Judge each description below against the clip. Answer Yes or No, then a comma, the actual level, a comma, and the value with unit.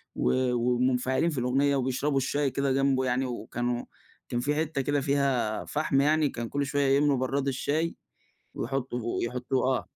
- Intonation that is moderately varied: No, narrow, 2.2 semitones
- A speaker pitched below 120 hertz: No, low, 135 Hz